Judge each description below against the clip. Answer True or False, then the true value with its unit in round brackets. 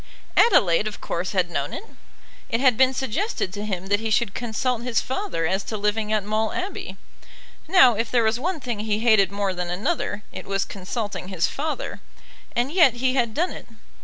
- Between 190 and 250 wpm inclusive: True (195 wpm)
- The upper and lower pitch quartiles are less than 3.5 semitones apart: False (4.3 semitones)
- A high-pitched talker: True (220 Hz)